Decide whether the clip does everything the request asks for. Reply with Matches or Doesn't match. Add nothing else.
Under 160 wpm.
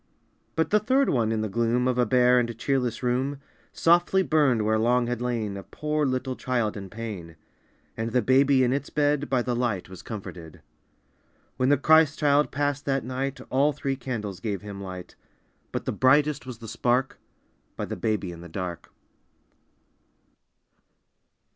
Doesn't match